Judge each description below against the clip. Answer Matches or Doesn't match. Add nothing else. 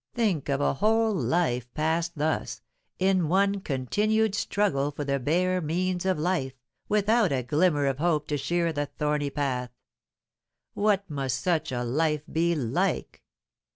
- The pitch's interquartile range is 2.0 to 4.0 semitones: Doesn't match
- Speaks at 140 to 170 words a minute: Matches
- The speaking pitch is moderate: Matches